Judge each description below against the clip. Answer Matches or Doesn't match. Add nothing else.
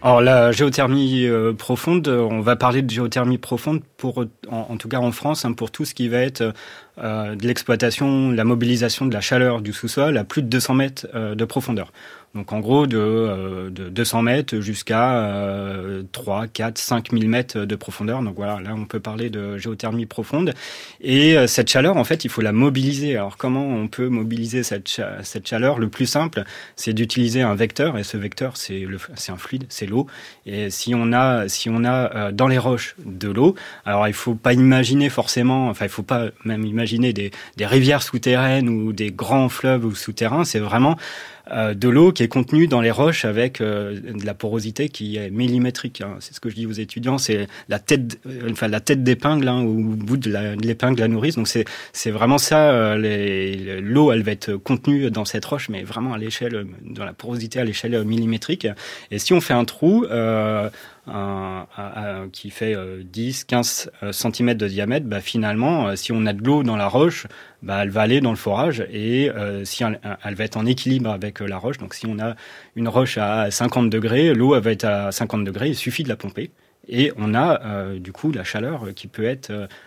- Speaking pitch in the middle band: Doesn't match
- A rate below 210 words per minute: Doesn't match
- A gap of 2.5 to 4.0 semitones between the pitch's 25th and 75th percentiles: Matches